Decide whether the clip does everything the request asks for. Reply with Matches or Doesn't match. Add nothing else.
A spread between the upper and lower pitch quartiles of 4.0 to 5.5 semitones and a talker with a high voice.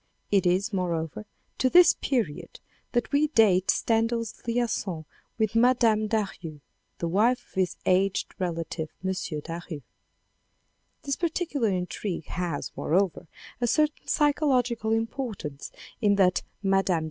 Matches